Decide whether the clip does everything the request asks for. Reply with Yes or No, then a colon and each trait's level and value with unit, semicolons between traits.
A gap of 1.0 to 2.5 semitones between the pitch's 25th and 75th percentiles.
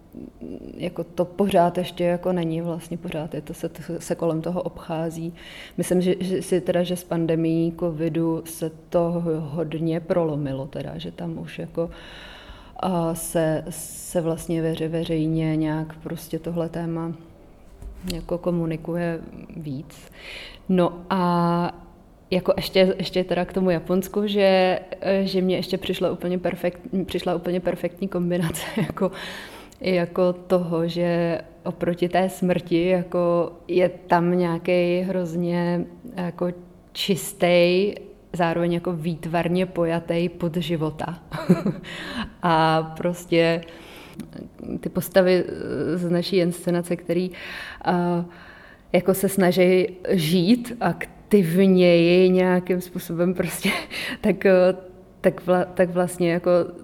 Yes: narrow, 1.6 semitones